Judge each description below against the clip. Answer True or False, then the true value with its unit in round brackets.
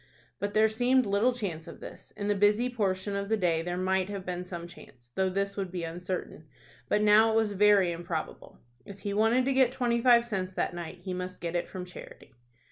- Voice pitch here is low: False (195 Hz)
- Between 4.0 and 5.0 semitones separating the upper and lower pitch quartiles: False (3.3 semitones)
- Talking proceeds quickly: True (220 wpm)